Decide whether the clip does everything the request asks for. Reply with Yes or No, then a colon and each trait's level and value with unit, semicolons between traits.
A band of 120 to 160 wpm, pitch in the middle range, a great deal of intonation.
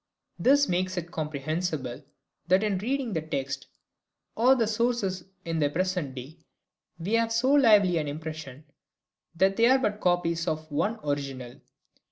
Yes: average, 150 wpm; medium, 175 Hz; wide, 5.9 semitones